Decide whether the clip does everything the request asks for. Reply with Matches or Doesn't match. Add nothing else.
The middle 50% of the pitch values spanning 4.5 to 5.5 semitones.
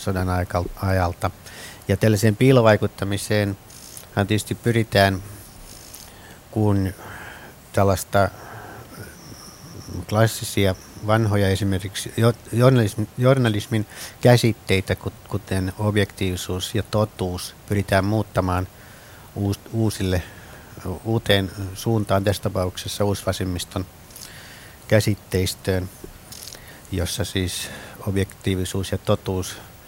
Doesn't match